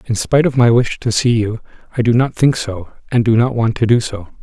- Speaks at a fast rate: Yes, fast, 270 wpm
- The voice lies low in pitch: Yes, low, 115 Hz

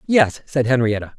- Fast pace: No, average, 150 wpm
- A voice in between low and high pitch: No, low, 130 Hz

